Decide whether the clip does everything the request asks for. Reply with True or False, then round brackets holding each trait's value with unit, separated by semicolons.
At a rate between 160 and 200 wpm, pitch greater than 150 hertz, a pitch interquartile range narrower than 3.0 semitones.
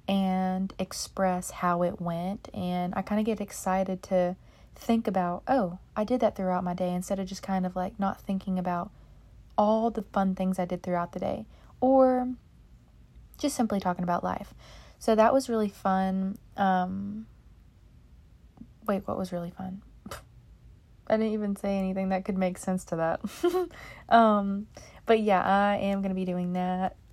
True (170 wpm; 190 Hz; 2.5 semitones)